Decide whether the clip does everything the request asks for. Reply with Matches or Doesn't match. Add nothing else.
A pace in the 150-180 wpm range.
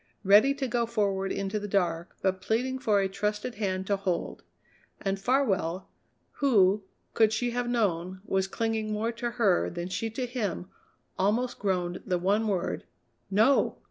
Matches